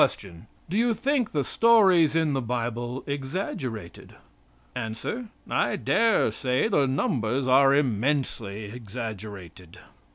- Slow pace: Yes, slow, 105 wpm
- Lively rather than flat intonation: Yes, wide, 6.3 semitones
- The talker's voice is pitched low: Yes, low, 130 Hz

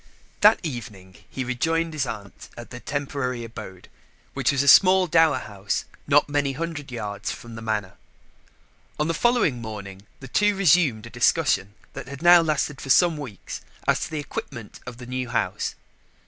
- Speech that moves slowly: No, average, 175 wpm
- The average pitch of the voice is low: Yes, low, 130 Hz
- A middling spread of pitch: No, wide, 5.9 semitones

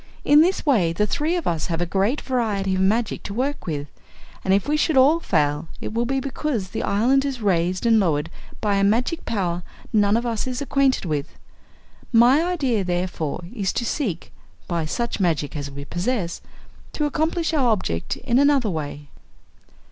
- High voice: Yes, high, 215 Hz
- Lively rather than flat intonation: Yes, wide, 7.4 semitones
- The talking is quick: No, average, 185 wpm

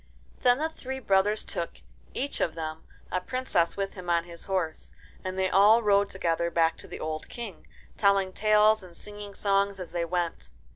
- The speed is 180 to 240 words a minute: Yes, average, 185 wpm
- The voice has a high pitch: Yes, high, 195 Hz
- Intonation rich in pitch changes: No, average, 3.6 semitones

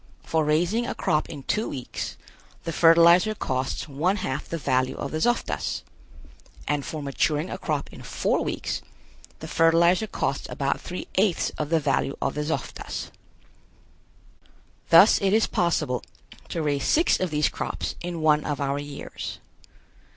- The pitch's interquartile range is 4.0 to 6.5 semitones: No, average, 3.6 semitones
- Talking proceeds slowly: No, average, 155 wpm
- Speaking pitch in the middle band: Yes, medium, 155 Hz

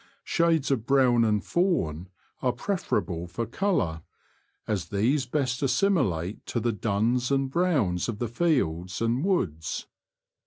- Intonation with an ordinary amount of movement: No, wide, 6.6 semitones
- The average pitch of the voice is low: Yes, low, 120 Hz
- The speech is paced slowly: Yes, slow, 130 wpm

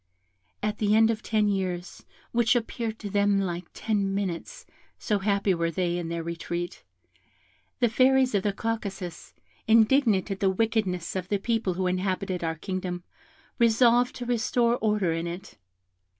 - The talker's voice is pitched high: Yes, high, 200 Hz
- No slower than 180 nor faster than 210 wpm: No, average, 155 wpm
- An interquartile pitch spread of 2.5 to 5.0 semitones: Yes, average, 3.7 semitones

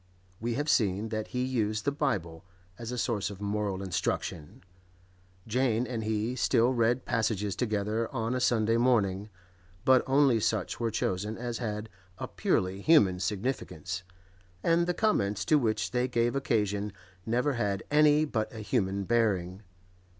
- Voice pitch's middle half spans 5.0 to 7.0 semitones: No, average, 3.6 semitones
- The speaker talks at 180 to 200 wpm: No, average, 150 wpm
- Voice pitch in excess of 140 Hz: No, low, 110 Hz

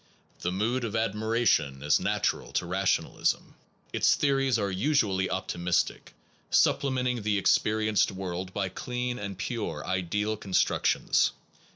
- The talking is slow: Yes, slow, 120 wpm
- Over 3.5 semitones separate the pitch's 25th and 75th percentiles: Yes, average, 4.0 semitones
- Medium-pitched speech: No, low, 105 Hz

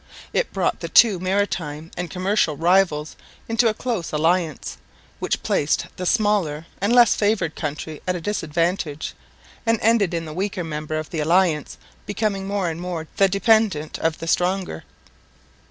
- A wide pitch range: No, average, 4.3 semitones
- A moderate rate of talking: Yes, average, 155 wpm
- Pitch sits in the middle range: Yes, medium, 180 Hz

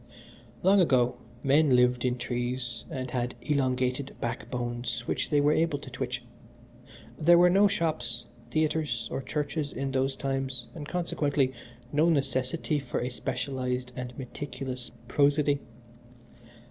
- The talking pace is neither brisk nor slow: No, slow, 130 wpm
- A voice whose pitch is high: No, low, 135 Hz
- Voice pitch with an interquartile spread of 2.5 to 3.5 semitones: Yes, average, 2.9 semitones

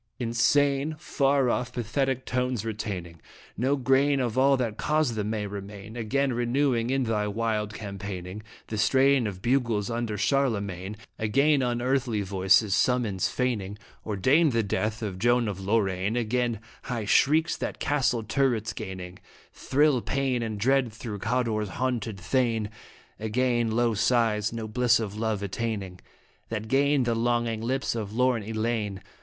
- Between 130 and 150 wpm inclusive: Yes, average, 145 wpm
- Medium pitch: No, low, 115 Hz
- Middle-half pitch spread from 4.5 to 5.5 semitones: No, average, 3.3 semitones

